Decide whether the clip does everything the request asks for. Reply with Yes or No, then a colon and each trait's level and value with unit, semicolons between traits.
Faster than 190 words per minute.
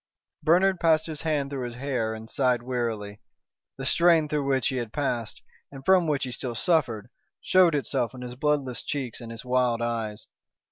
No: average, 185 wpm